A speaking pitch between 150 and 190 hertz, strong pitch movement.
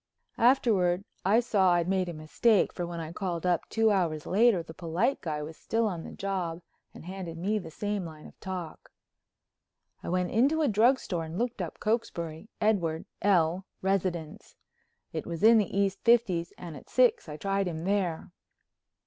No: medium, 185 Hz; average, 4.1 semitones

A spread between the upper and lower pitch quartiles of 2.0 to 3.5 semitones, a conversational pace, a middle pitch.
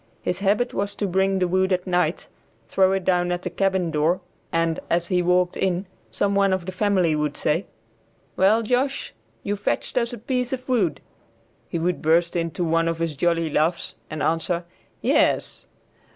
Yes: average, 3.0 semitones; average, 180 wpm; medium, 180 Hz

